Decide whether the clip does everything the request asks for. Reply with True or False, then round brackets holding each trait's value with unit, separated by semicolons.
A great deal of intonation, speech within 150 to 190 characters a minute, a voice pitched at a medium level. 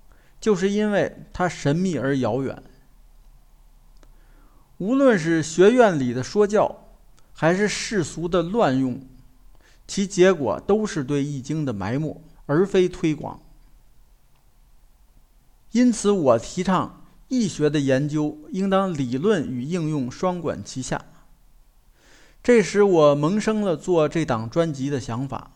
True (5.9 semitones; 180 characters per minute; 165 Hz)